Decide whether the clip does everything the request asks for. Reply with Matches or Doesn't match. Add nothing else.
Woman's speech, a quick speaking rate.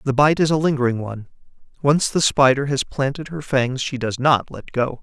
Doesn't match